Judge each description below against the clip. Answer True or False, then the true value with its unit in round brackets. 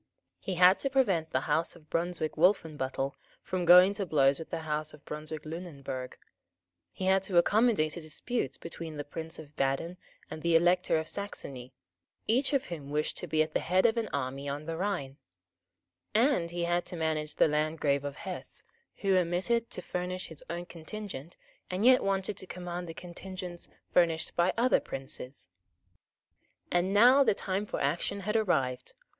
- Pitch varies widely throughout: False (3.8 semitones)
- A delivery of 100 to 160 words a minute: False (175 wpm)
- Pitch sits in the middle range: True (170 Hz)